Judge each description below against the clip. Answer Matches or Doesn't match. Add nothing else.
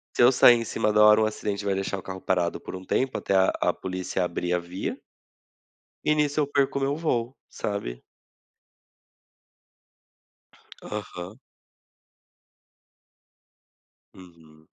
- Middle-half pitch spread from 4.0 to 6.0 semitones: Matches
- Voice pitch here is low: Matches